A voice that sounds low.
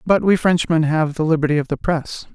No: medium, 160 Hz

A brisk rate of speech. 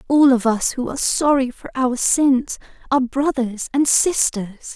No: average, 165 wpm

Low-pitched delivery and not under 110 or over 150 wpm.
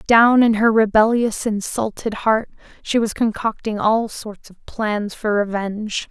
No: high, 215 Hz; average, 145 wpm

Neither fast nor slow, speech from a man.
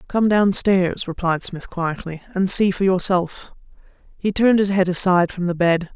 No: average, 170 wpm; female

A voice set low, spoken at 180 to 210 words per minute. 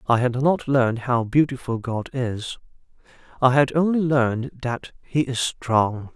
No: low, 130 Hz; average, 155 wpm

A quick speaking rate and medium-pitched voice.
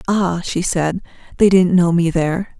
No: average, 185 wpm; medium, 175 Hz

